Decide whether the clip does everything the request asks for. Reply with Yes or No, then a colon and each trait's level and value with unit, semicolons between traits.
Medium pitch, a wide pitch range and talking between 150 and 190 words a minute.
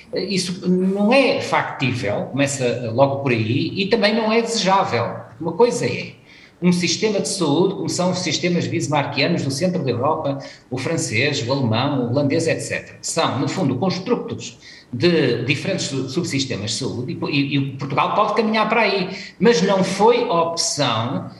Yes: medium, 165 Hz; wide, 5.9 semitones; average, 155 wpm